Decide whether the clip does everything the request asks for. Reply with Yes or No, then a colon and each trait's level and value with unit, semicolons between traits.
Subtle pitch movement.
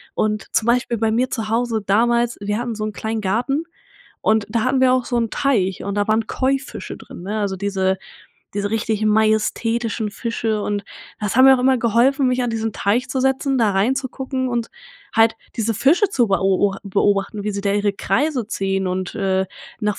No: average, 3.4 semitones